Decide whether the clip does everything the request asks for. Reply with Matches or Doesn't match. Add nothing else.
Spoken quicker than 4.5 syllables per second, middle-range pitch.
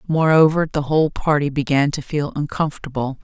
Matches